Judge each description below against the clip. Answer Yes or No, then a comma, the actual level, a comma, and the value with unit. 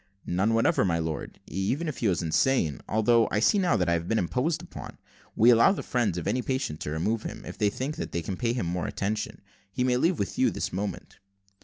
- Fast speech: Yes, fast, 235 wpm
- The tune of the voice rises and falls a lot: Yes, wide, 6.1 semitones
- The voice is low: Yes, low, 110 Hz